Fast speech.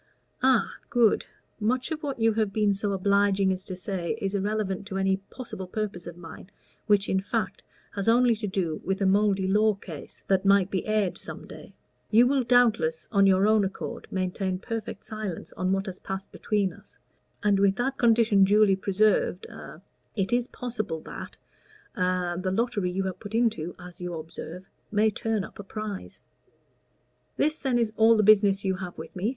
No: average, 185 wpm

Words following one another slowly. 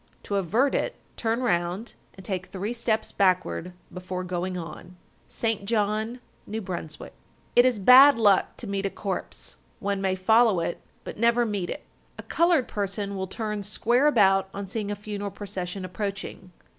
No: average, 165 wpm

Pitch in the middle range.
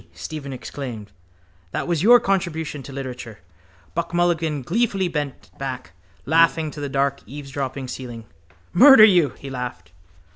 Yes: medium, 145 Hz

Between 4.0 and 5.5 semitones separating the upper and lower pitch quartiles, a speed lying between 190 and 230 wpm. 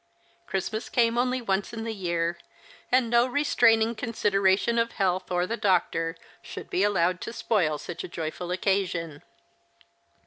No: average, 4.5 semitones; average, 145 wpm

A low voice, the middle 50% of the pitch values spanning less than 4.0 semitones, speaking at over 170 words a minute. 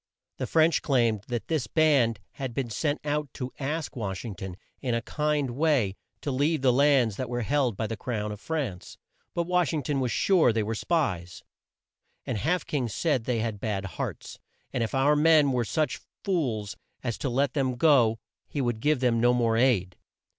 No: low, 125 Hz; average, 4.7 semitones; average, 195 wpm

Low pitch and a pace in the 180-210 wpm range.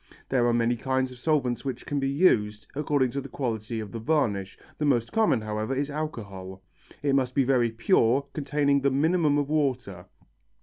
Yes: low, 130 Hz; average, 185 wpm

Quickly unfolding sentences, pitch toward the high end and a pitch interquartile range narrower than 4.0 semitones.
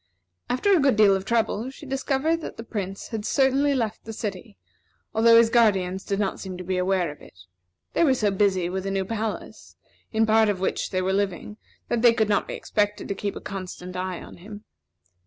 Yes: fast, 215 wpm; high, 210 Hz; average, 3.4 semitones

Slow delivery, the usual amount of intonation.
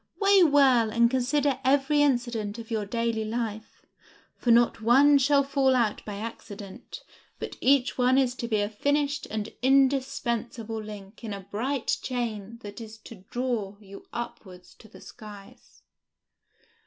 No: average, 150 wpm; average, 3.7 semitones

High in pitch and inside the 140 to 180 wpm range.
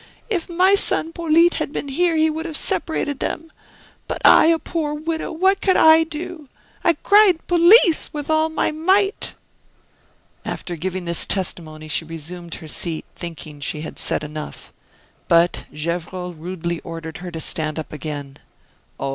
Yes: very high, 270 Hz; average, 160 wpm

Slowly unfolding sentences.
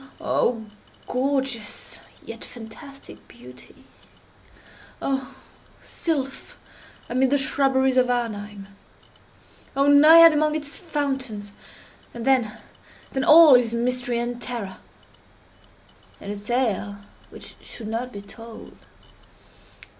Yes: slow, 95 wpm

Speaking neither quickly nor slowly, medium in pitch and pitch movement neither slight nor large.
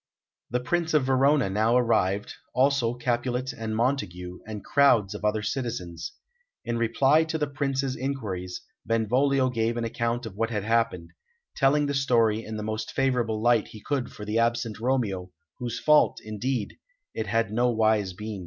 No: average, 165 wpm; low, 115 Hz; average, 3.5 semitones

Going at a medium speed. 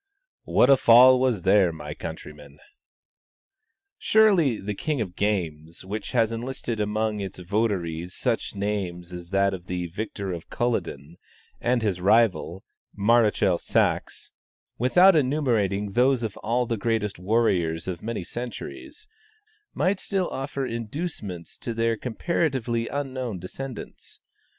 No: slow, 125 wpm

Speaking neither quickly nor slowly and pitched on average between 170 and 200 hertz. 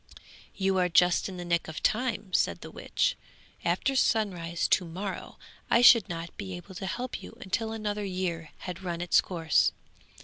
Yes: average, 175 wpm; medium, 185 Hz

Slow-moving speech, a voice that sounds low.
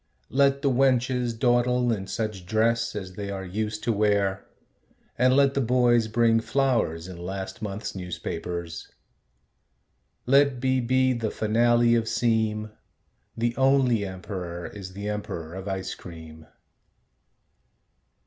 Yes: slow, 130 wpm; low, 110 Hz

